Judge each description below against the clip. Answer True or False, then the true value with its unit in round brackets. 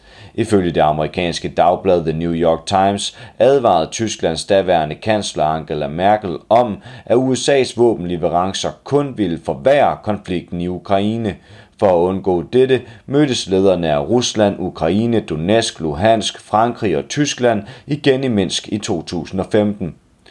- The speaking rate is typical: False (125 wpm)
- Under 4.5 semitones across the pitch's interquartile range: False (5.2 semitones)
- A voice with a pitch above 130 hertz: False (105 Hz)